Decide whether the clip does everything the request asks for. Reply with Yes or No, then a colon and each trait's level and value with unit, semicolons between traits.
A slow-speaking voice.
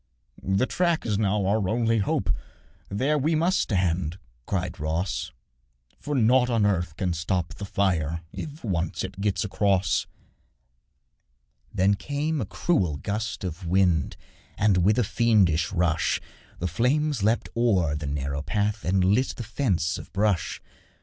No: average, 145 wpm